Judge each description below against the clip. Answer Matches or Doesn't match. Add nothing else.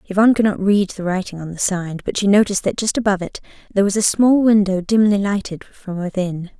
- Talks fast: Matches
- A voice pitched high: Matches